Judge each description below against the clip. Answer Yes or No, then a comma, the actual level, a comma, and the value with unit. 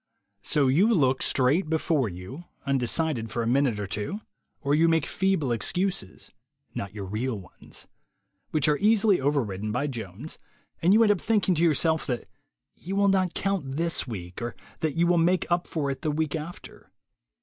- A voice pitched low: No, medium, 150 Hz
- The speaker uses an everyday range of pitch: No, wide, 6.3 semitones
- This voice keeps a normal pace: Yes, average, 180 wpm